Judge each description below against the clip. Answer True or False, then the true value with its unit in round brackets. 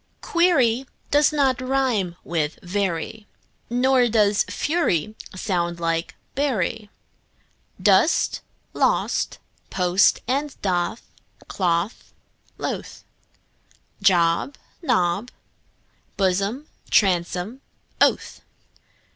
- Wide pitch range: True (6.6 semitones)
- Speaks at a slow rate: True (75 wpm)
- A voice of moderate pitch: False (205 Hz)